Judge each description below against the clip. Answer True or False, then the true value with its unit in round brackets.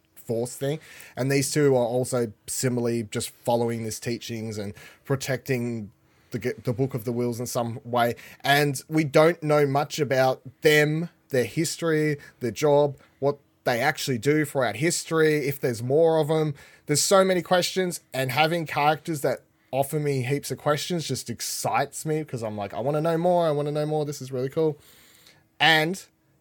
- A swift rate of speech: False (180 wpm)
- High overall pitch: False (140 Hz)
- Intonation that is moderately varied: True (3.8 semitones)